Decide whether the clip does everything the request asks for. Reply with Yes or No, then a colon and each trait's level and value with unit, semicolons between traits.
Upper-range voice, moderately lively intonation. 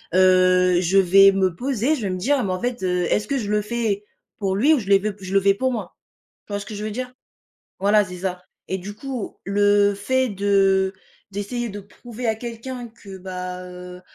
Yes: high, 200 Hz; average, 3.4 semitones